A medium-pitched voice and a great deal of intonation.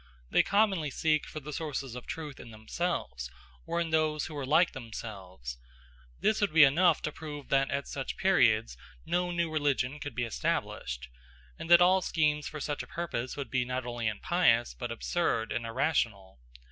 Yes: medium, 145 Hz; wide, 5.7 semitones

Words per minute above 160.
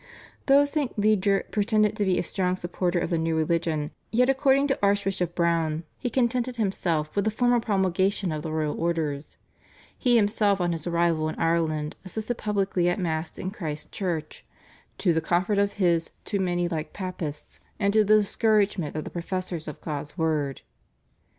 Yes: average, 175 wpm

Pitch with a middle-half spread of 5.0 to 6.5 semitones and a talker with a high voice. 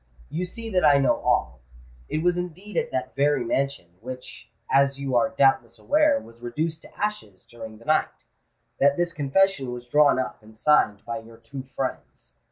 No: wide, 5.4 semitones; low, 135 Hz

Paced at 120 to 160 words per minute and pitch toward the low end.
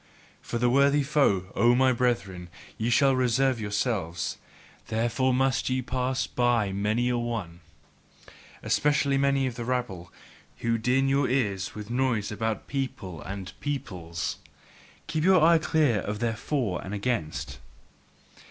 Yes: average, 140 wpm; low, 120 Hz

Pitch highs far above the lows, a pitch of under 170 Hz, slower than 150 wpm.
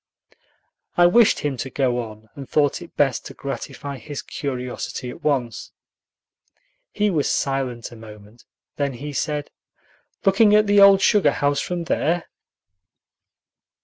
Yes: wide, 5.7 semitones; medium, 140 Hz; average, 140 wpm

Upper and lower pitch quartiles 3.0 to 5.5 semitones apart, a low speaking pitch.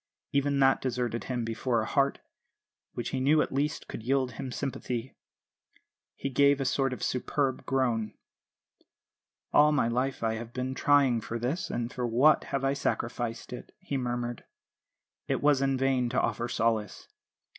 No: narrow, 2.5 semitones; low, 130 Hz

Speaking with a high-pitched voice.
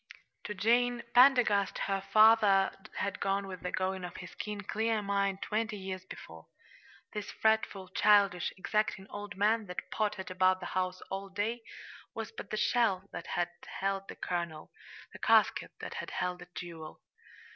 Yes: high, 195 Hz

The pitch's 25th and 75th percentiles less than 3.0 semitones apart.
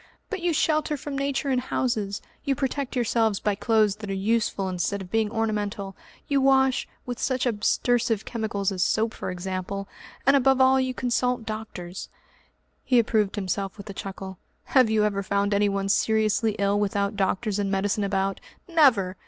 No: average, 4.1 semitones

